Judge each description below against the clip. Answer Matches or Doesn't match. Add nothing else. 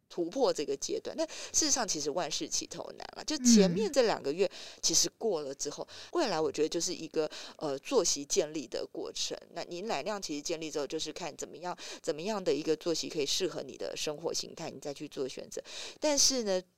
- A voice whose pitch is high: Matches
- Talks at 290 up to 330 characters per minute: Matches